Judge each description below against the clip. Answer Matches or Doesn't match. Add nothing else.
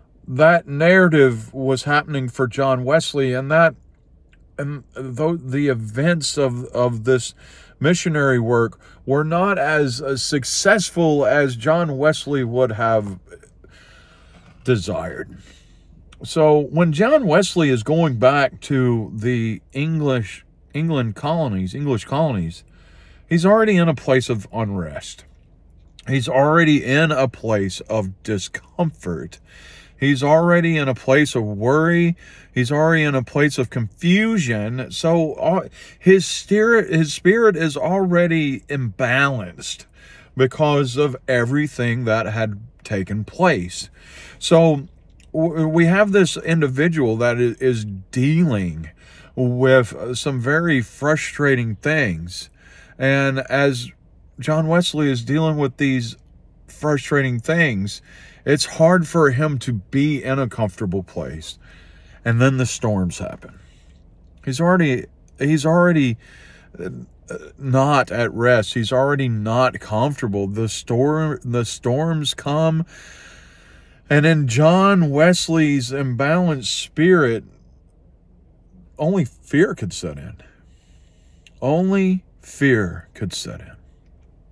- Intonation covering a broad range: Matches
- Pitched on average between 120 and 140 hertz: Matches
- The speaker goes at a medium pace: Doesn't match